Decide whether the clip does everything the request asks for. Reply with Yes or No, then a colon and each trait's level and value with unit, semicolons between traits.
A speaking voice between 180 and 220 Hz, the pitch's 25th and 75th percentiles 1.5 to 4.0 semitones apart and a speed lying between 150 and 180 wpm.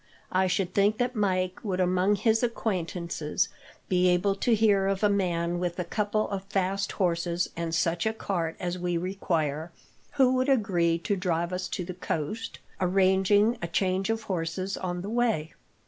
Yes: medium, 185 Hz; average, 2.8 semitones; average, 175 wpm